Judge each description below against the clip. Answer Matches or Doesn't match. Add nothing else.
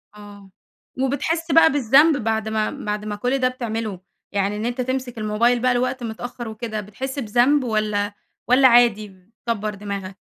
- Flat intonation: Doesn't match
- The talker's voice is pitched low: Doesn't match